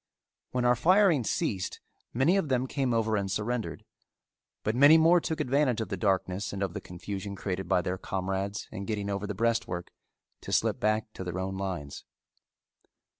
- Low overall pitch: Yes, low, 105 Hz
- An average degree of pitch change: Yes, average, 4.6 semitones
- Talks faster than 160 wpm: Yes, average, 175 wpm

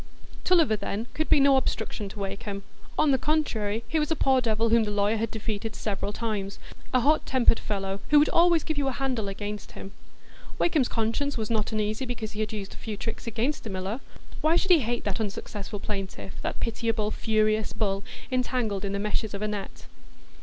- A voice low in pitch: No, high, 220 Hz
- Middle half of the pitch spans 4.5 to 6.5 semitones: No, average, 3.9 semitones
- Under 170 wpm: No, fast, 205 wpm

